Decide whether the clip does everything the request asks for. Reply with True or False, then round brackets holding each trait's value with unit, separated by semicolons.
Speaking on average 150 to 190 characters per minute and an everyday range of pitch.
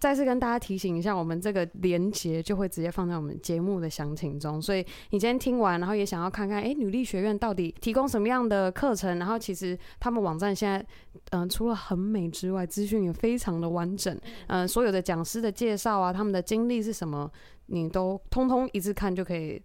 False (350 characters per minute; 3.7 semitones)